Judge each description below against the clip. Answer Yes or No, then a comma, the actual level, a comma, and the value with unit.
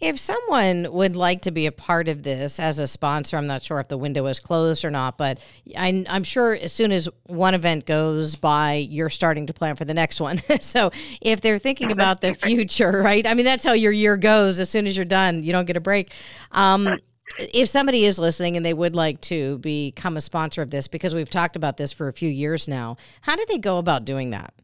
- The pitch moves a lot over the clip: No, average, 4.5 semitones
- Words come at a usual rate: No, fast, 240 wpm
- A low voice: No, medium, 170 Hz